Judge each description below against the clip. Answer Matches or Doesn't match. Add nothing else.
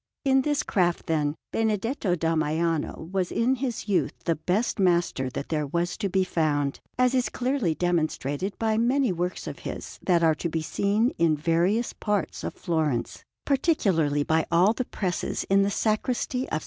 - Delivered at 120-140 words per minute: Doesn't match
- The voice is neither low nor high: Matches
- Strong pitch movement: Matches